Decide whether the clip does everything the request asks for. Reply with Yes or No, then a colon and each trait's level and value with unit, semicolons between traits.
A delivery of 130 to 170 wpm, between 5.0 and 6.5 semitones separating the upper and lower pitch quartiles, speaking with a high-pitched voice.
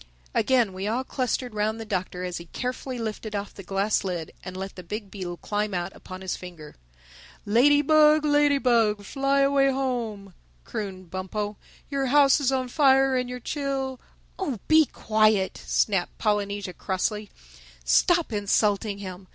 Yes: average, 150 wpm; wide, 5.5 semitones; high, 215 Hz